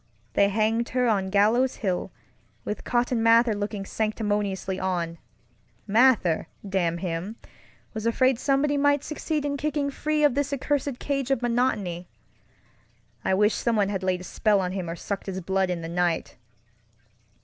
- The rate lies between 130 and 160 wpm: Yes, average, 150 wpm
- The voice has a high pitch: Yes, high, 215 Hz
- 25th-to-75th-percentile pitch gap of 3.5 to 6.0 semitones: Yes, average, 5.3 semitones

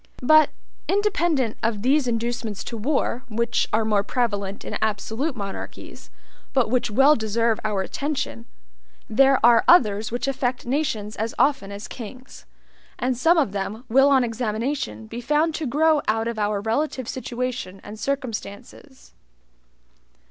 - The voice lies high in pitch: Yes, high, 240 Hz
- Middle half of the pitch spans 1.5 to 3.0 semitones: No, average, 4.1 semitones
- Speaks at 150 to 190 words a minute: No, average, 140 wpm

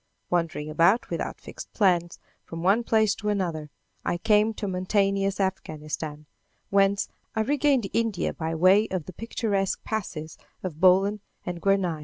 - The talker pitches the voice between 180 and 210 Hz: Yes, high, 190 Hz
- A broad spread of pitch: No, average, 3.6 semitones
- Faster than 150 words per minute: No, average, 145 wpm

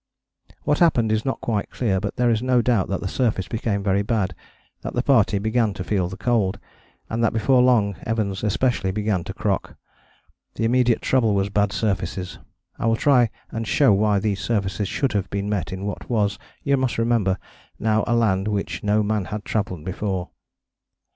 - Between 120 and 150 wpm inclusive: No, average, 190 wpm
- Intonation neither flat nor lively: Yes, average, 3.0 semitones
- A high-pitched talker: No, low, 105 Hz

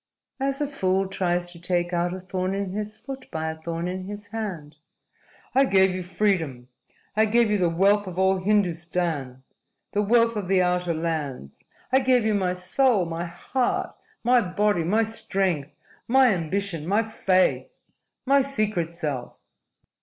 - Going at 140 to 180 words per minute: Yes, average, 160 wpm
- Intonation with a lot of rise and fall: No, average, 3.7 semitones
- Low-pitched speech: No, medium, 185 Hz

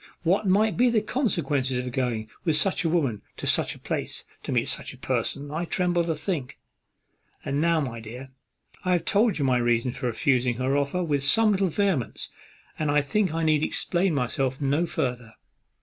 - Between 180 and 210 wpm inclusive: Yes, average, 195 wpm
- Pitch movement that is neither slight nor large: No, wide, 5.8 semitones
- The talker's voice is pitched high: No, medium, 150 Hz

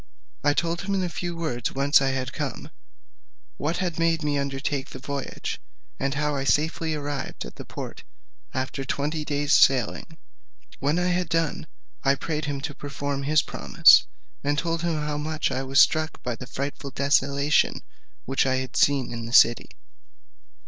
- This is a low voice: No, medium, 145 Hz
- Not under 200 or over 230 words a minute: No, average, 175 wpm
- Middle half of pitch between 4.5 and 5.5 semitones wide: No, narrow, 2.6 semitones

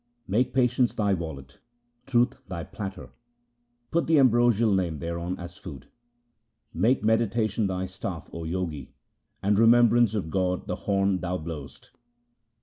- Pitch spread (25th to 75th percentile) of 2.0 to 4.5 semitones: No, average, 5.2 semitones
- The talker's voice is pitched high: No, very low, 95 Hz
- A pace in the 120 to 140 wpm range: Yes, slow, 135 wpm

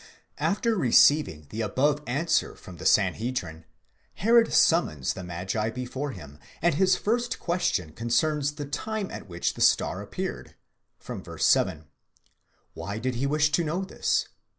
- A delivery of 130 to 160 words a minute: Yes, average, 145 wpm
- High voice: No, medium, 140 Hz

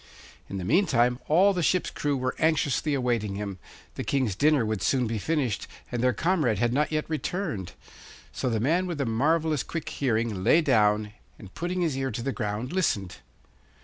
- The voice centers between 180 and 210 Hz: No, low, 130 Hz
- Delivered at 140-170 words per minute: No, average, 185 wpm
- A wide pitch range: Yes, wide, 6.3 semitones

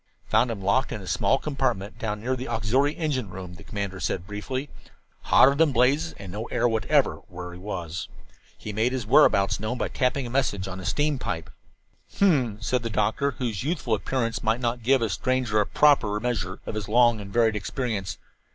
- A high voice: No, low, 115 Hz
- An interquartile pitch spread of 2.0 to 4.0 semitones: No, average, 4.4 semitones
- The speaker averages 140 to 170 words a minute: No, average, 195 wpm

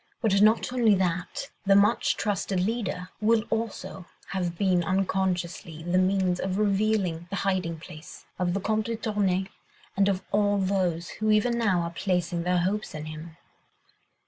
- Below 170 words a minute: Yes, average, 160 wpm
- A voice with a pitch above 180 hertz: Yes, high, 190 Hz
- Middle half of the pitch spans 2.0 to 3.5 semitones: Yes, average, 2.8 semitones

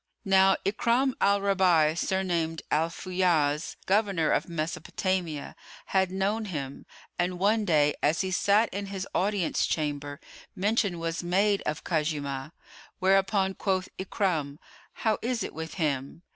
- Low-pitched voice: No, medium, 185 Hz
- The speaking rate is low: Yes, slow, 130 wpm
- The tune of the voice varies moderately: Yes, average, 3.8 semitones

